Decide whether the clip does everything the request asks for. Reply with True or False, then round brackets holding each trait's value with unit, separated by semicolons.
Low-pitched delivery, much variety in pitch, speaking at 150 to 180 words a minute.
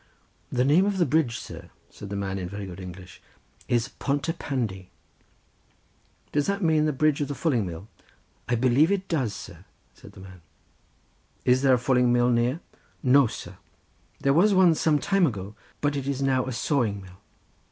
False (130 Hz; 6.7 semitones; 190 wpm)